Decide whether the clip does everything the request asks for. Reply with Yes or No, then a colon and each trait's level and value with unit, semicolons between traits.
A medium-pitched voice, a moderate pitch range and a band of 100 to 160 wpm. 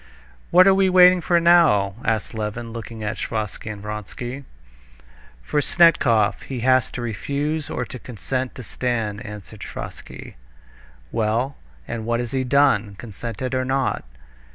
No: low, 120 Hz; average, 4.4 semitones; average, 145 wpm